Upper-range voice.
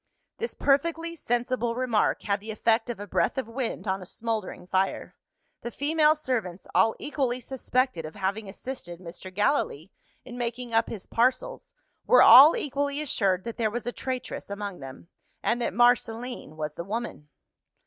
Yes: high, 235 Hz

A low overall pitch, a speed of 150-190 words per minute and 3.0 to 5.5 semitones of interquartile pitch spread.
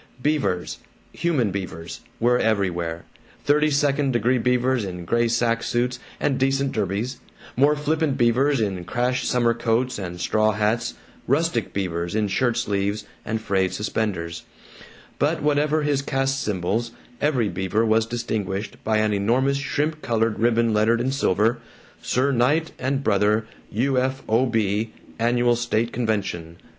No: low, 115 Hz; average, 140 wpm; average, 4.1 semitones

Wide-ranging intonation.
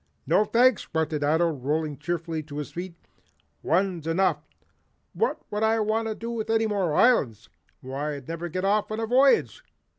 Yes: wide, 6.2 semitones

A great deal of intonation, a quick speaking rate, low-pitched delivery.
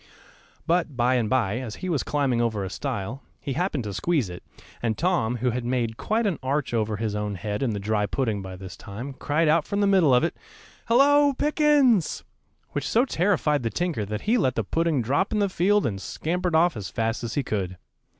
Yes: wide, 8.1 semitones; fast, 220 wpm; low, 130 Hz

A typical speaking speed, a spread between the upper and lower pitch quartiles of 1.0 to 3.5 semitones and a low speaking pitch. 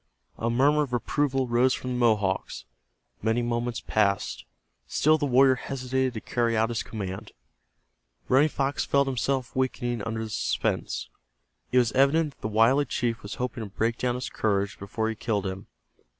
Yes: average, 170 wpm; average, 2.9 semitones; low, 120 Hz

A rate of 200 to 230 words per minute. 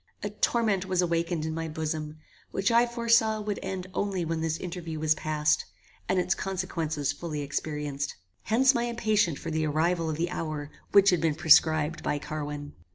No: average, 175 wpm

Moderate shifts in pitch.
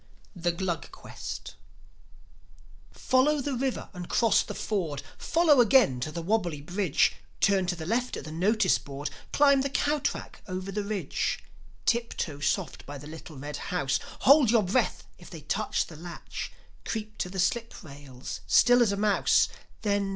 No: wide, 6.8 semitones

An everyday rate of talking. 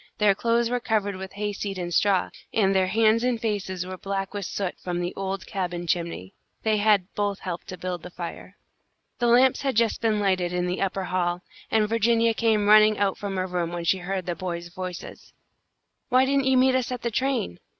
No: fast, 210 wpm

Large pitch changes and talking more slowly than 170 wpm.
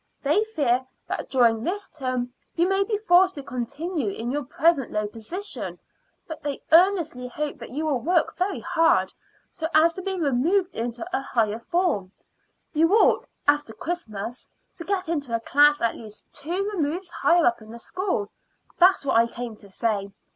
No: wide, 6.9 semitones; average, 180 wpm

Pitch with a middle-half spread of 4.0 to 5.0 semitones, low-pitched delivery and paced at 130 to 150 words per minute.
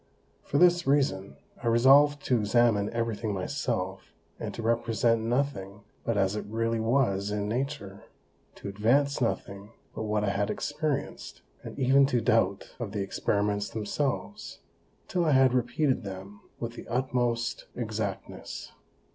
Yes: average, 4.5 semitones; low, 115 Hz; average, 145 wpm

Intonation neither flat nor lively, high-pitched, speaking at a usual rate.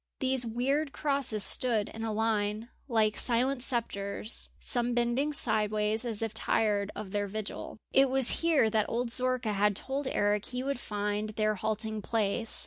Yes: average, 3.2 semitones; high, 225 Hz; average, 160 wpm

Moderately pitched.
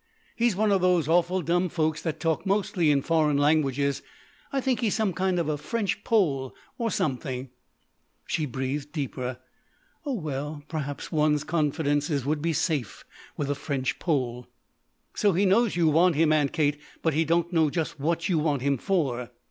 Yes: medium, 155 Hz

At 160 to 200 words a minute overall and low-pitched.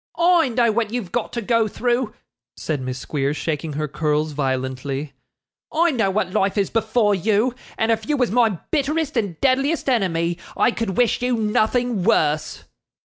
No: average, 170 wpm; high, 215 Hz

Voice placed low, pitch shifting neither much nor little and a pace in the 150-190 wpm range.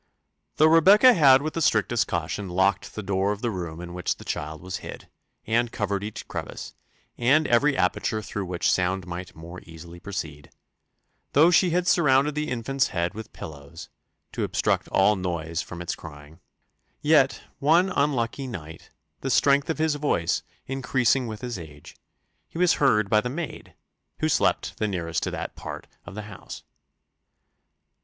No: low, 105 Hz; wide, 7.8 semitones; average, 165 wpm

